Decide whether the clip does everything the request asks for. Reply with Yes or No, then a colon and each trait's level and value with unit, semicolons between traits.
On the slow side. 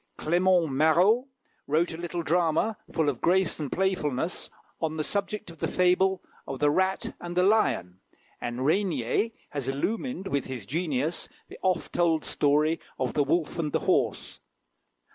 No: average, 160 wpm